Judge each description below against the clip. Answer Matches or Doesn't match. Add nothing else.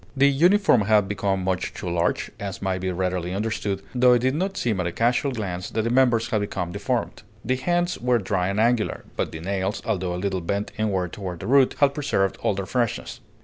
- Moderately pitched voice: Doesn't match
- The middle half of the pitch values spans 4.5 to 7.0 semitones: Matches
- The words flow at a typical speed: Doesn't match